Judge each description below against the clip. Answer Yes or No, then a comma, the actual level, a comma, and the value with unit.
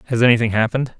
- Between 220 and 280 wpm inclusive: Yes, fast, 240 wpm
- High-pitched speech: No, low, 120 Hz